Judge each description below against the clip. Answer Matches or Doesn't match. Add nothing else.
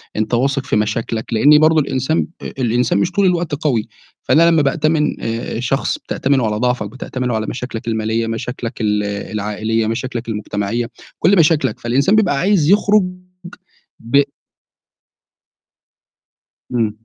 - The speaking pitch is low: Matches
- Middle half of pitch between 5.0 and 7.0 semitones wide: Matches